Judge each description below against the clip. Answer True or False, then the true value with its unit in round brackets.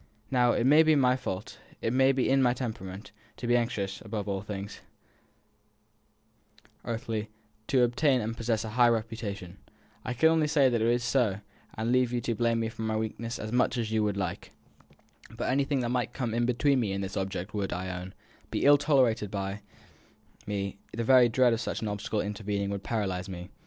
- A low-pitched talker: True (115 Hz)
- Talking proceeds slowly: False (200 wpm)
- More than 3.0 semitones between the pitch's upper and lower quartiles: True (3.5 semitones)